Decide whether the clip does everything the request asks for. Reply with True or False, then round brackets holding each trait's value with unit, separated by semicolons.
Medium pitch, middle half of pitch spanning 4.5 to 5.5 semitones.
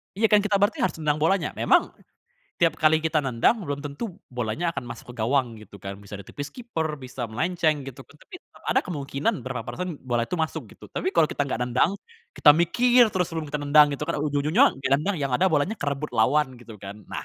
True (150 Hz; 5.1 semitones)